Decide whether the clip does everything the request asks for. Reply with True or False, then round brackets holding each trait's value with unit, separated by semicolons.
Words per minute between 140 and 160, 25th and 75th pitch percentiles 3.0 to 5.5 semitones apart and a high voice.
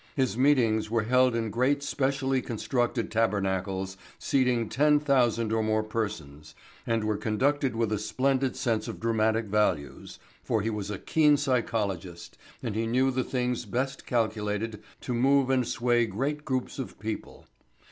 False (155 wpm; 3.4 semitones; 115 Hz)